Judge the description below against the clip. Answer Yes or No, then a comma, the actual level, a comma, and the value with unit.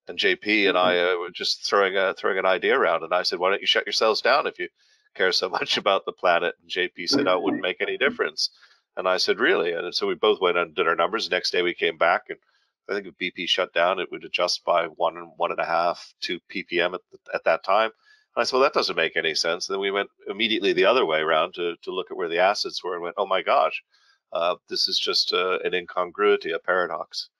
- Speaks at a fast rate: Yes, fast, 265 wpm